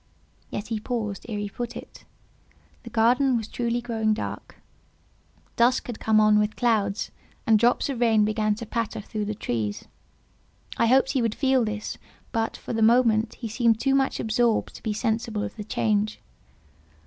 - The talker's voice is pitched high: Yes, high, 225 Hz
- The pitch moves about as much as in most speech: No, narrow, 2.1 semitones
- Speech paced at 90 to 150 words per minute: No, average, 175 wpm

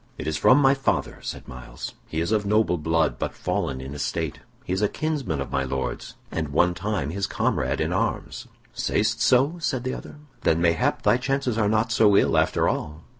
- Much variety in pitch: Yes, wide, 7.9 semitones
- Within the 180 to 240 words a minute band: Yes, fast, 205 wpm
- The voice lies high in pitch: No, low, 100 Hz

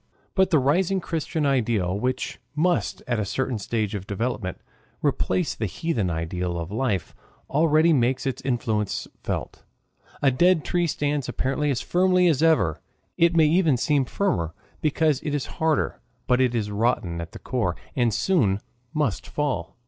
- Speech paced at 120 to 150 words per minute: No, average, 160 wpm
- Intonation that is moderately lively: No, wide, 7.0 semitones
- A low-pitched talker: Yes, low, 130 Hz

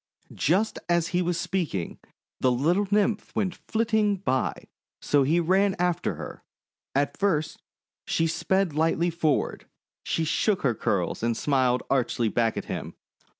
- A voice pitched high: No, medium, 165 Hz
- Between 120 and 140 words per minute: No, average, 150 wpm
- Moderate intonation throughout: No, wide, 5.9 semitones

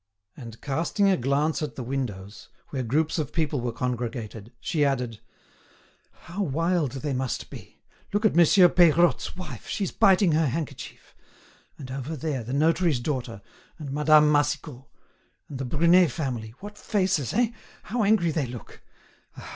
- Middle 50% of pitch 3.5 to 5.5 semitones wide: Yes, average, 4.9 semitones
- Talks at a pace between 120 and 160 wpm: Yes, average, 150 wpm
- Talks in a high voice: No, medium, 145 Hz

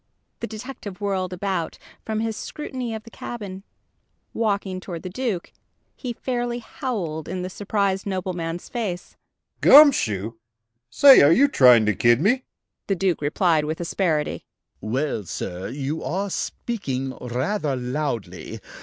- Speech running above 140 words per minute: No, slow, 135 wpm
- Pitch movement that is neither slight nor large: No, wide, 6.6 semitones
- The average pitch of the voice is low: No, medium, 185 Hz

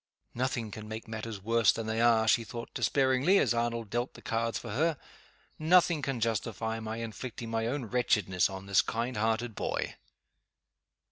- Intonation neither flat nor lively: No, narrow, 1.7 semitones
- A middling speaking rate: Yes, average, 165 wpm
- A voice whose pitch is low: Yes, low, 115 Hz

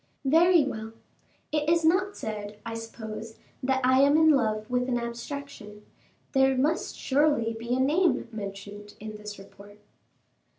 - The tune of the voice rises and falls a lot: No, average, 5.0 semitones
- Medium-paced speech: Yes, average, 145 wpm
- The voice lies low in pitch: No, high, 245 Hz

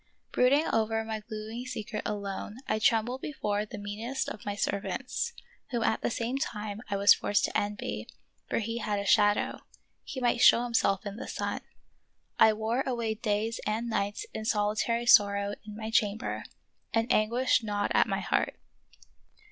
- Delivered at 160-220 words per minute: Yes, average, 170 wpm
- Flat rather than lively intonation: Yes, narrow, 2.2 semitones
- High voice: Yes, high, 220 Hz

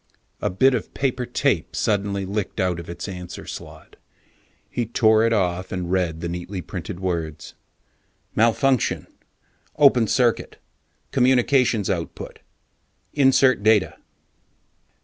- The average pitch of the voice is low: Yes, low, 105 Hz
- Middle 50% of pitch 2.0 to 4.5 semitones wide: No, average, 5.3 semitones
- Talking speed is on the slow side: Yes, slow, 115 wpm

